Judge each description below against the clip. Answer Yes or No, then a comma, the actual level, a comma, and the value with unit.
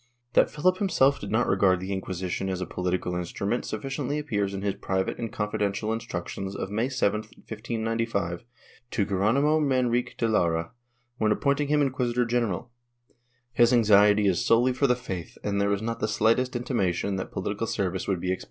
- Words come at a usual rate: Yes, average, 175 wpm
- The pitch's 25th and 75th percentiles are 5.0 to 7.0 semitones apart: No, average, 4.2 semitones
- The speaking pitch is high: No, low, 105 Hz